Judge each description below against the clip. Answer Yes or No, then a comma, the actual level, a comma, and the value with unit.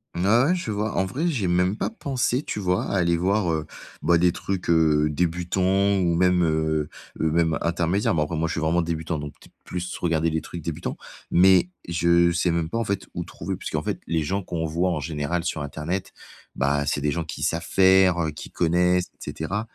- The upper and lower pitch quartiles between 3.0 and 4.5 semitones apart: No, narrow, 2.6 semitones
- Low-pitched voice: Yes, very low, 85 Hz